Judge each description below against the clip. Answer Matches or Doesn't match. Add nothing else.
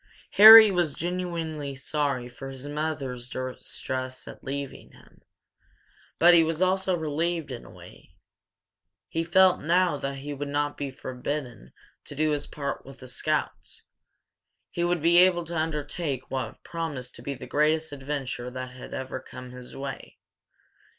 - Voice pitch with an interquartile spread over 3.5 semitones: Matches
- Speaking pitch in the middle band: Matches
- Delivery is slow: Doesn't match